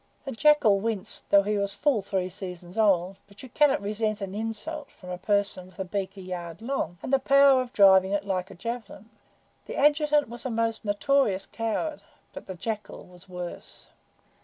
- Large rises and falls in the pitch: No, average, 4.2 semitones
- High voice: Yes, high, 205 Hz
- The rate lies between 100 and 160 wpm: No, average, 190 wpm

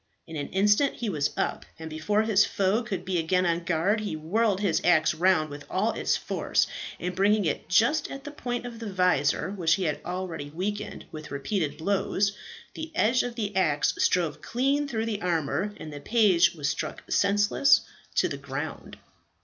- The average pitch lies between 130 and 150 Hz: No, high, 190 Hz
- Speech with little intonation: No, average, 5.0 semitones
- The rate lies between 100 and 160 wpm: No, average, 190 wpm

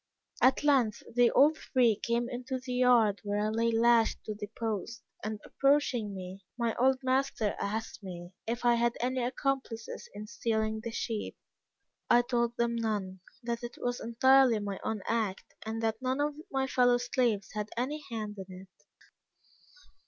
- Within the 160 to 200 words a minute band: Yes, average, 165 wpm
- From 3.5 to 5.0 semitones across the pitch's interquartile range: No, average, 2.7 semitones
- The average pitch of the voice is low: No, high, 235 Hz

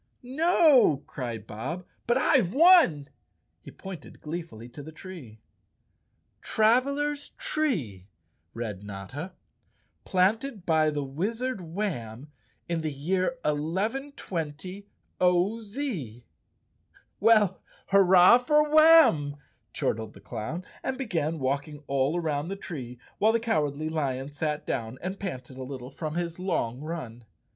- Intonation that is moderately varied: No, wide, 7.7 semitones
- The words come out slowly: Yes, slow, 130 wpm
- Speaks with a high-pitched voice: No, medium, 165 Hz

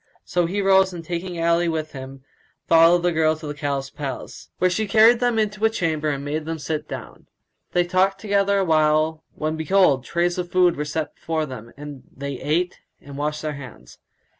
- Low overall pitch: No, medium, 160 Hz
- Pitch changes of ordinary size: Yes, average, 3.5 semitones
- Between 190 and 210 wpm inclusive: Yes, average, 195 wpm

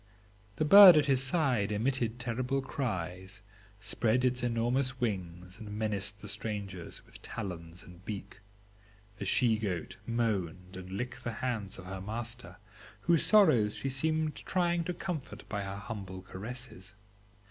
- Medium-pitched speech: No, low, 110 Hz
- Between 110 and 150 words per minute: Yes, average, 145 wpm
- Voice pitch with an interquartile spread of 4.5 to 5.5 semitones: Yes, average, 5.0 semitones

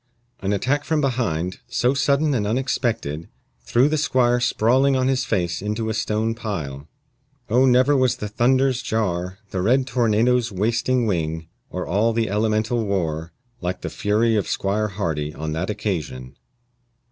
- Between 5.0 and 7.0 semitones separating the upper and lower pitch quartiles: Yes, wide, 5.4 semitones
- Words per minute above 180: No, average, 155 wpm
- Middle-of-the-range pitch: No, low, 110 Hz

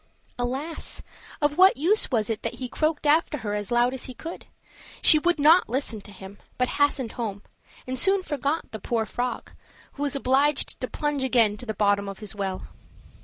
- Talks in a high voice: Yes, very high, 255 Hz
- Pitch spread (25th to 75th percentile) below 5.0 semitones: No, average, 5.3 semitones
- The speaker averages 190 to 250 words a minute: Yes, average, 195 wpm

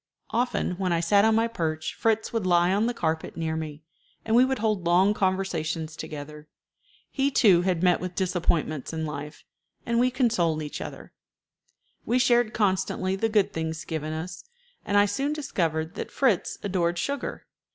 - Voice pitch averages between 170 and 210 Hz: Yes, medium, 185 Hz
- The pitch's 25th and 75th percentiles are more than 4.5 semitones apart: Yes, wide, 5.6 semitones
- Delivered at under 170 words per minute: No, average, 175 wpm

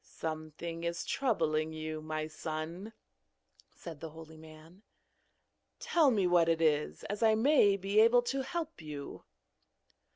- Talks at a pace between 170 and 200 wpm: No, slow, 135 wpm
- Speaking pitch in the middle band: Yes, medium, 165 Hz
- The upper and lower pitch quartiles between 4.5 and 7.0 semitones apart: Yes, wide, 5.5 semitones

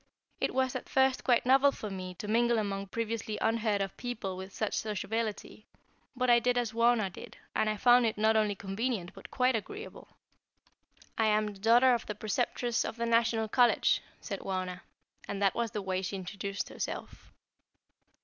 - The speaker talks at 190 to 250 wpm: No, average, 180 wpm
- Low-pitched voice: No, high, 220 Hz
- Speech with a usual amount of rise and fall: Yes, average, 3.2 semitones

